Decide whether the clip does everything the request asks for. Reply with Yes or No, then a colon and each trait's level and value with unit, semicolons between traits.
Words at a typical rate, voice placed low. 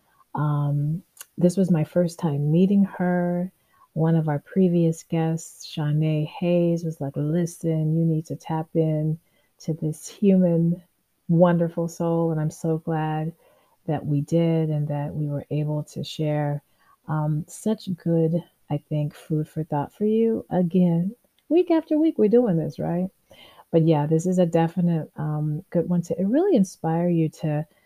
No: average, 160 wpm; medium, 165 Hz